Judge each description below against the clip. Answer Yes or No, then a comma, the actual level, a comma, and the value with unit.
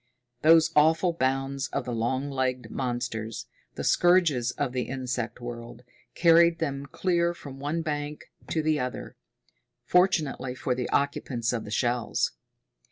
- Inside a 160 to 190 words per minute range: No, average, 140 wpm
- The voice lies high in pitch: No, low, 135 Hz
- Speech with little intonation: No, average, 4.4 semitones